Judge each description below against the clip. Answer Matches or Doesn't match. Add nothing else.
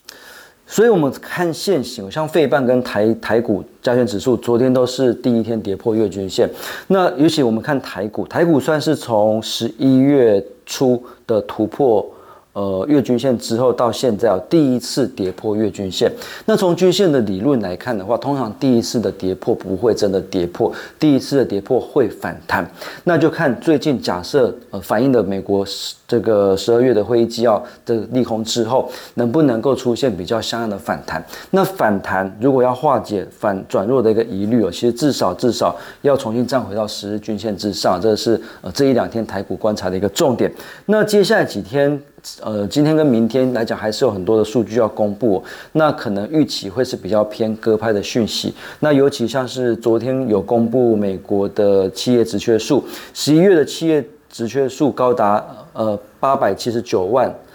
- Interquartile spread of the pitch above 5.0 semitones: Doesn't match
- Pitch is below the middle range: Matches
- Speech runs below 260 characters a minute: Doesn't match